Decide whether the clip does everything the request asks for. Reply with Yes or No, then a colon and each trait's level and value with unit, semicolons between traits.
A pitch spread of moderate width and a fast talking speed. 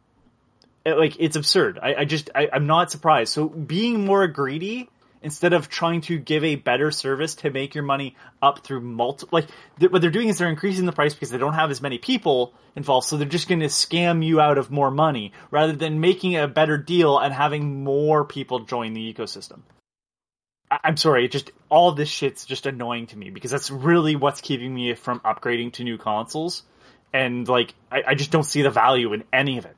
Yes: average, 3.2 semitones; fast, 210 wpm